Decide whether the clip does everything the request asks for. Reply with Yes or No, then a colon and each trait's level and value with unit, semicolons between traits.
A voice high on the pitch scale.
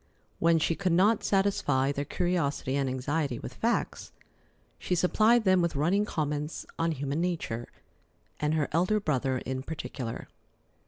No: medium, 160 Hz